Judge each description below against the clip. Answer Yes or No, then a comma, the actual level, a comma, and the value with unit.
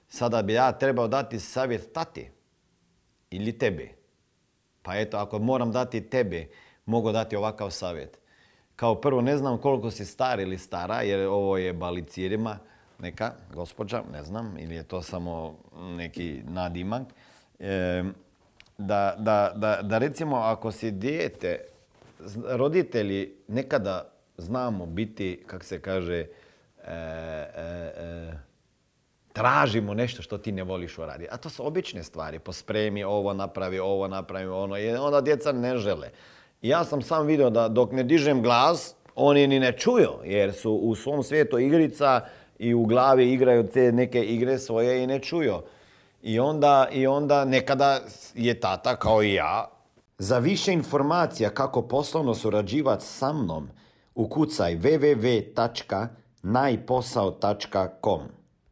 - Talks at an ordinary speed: Yes, average, 140 wpm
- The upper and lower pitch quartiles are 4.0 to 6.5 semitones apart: Yes, average, 5.2 semitones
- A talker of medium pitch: No, low, 115 Hz